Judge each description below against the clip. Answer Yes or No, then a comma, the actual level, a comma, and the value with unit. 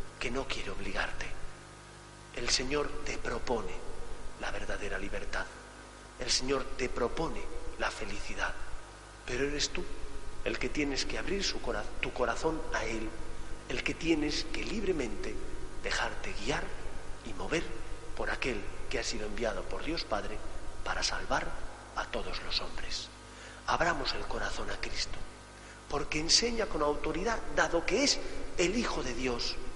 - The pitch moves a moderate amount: No, wide, 5.9 semitones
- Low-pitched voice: Yes, low, 125 Hz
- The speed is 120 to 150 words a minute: Yes, average, 145 wpm